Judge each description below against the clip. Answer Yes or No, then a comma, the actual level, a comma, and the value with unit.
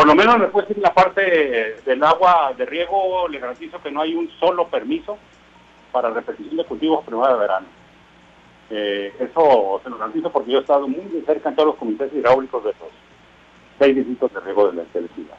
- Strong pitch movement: Yes, wide, 7.0 semitones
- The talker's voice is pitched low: No, medium, 155 Hz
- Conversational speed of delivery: No, fast, 200 wpm